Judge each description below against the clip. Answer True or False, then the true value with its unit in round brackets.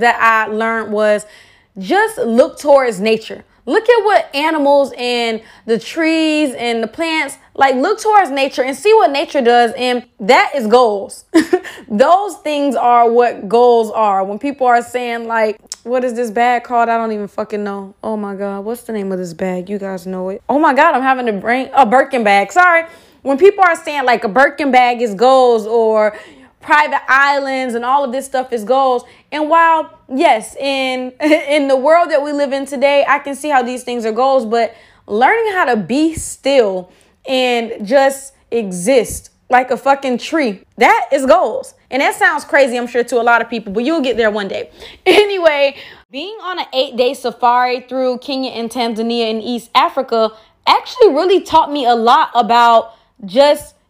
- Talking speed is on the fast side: True (190 wpm)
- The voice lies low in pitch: False (255 Hz)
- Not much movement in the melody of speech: False (4.2 semitones)